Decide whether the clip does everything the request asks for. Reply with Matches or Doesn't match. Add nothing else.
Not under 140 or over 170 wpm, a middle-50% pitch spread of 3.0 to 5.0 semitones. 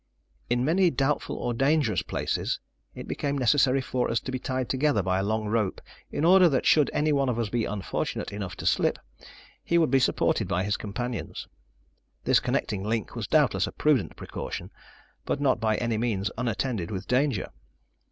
Doesn't match